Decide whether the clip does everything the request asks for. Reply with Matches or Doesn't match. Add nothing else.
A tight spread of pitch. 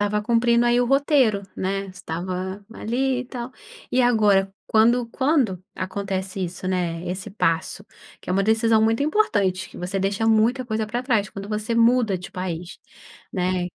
Doesn't match